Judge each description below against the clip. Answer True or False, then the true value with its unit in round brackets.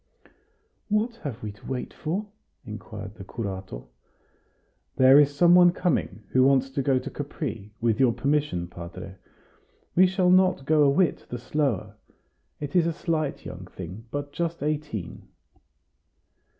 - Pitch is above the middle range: False (140 Hz)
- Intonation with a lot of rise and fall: True (7.0 semitones)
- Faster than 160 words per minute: False (150 wpm)